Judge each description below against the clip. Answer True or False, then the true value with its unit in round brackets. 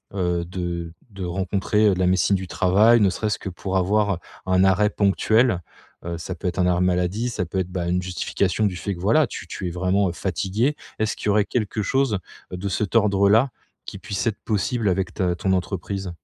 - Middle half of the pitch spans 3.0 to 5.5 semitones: False (2.6 semitones)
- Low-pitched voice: True (95 Hz)